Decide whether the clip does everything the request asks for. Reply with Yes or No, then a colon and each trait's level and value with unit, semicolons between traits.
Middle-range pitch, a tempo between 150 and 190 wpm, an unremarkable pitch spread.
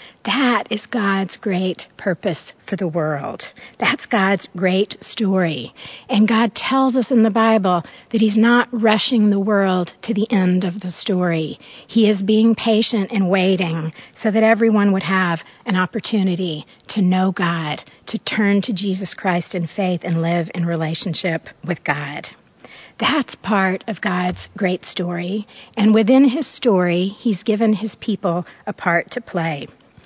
No: high, 195 Hz; average, 155 wpm; average, 3.7 semitones